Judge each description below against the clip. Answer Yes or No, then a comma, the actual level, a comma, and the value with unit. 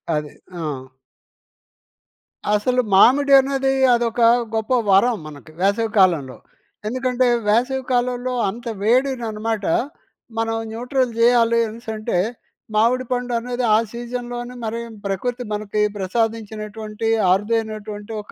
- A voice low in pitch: No, high, 230 Hz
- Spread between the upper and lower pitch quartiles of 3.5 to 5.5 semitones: No, average, 2.7 semitones